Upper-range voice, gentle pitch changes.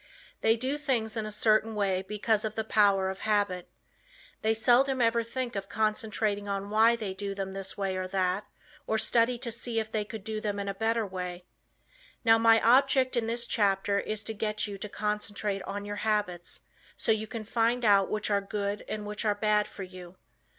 Yes: high, 210 Hz; narrow, 2.1 semitones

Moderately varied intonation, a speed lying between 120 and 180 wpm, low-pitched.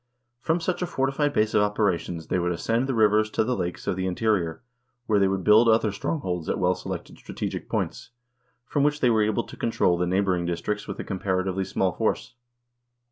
No: average, 4.0 semitones; fast, 205 wpm; low, 105 Hz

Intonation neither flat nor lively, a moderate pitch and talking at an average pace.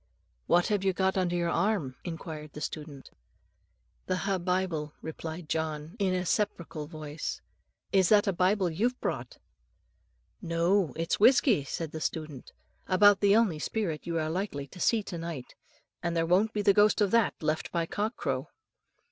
Yes: average, 4.0 semitones; medium, 175 Hz; average, 170 wpm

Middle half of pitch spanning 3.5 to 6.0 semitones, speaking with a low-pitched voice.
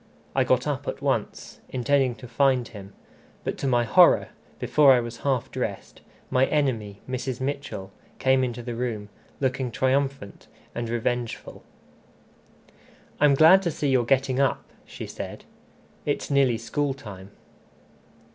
No: average, 2.7 semitones; low, 130 Hz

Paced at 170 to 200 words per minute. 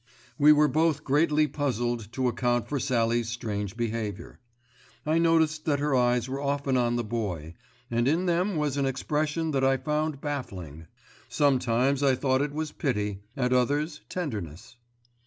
No: average, 155 wpm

